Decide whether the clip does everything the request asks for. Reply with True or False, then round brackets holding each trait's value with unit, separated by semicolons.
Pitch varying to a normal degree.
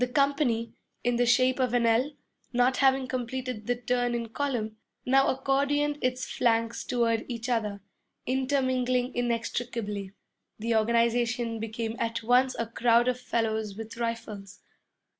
False (1.9 semitones)